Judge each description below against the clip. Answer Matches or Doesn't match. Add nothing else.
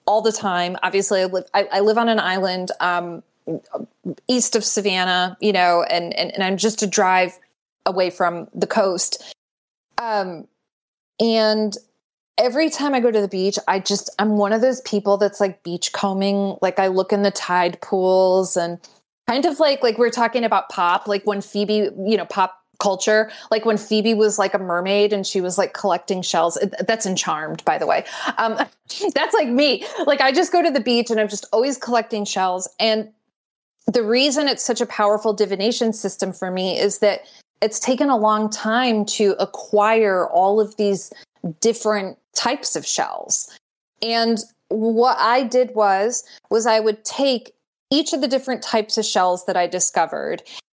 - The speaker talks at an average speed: Matches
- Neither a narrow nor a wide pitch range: Matches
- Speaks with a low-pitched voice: Doesn't match